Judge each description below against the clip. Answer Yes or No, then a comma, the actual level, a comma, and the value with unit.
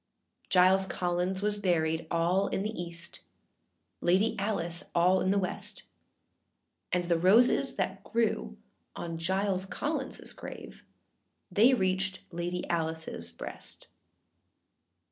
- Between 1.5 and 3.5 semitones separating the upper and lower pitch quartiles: Yes, narrow, 2.5 semitones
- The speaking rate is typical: No, slow, 115 wpm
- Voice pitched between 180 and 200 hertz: Yes, medium, 185 Hz